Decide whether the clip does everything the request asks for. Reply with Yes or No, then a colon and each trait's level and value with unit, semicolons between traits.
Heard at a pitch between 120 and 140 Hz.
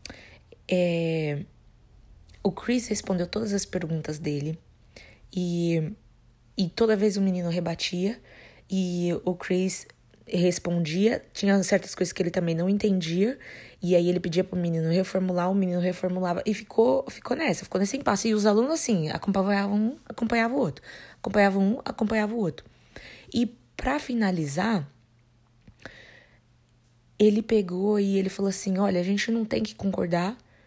No: medium, 185 Hz